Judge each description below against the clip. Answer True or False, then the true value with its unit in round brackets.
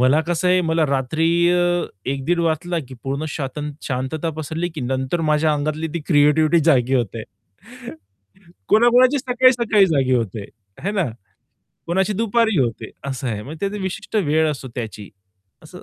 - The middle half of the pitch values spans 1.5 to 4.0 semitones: False (5.4 semitones)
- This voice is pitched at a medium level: True (155 Hz)